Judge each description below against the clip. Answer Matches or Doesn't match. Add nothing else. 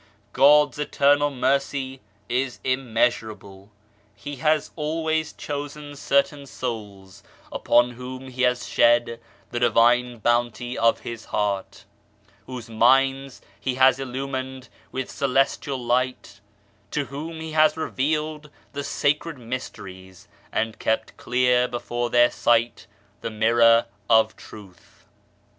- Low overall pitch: Matches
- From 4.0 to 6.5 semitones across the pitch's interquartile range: Doesn't match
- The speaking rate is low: Matches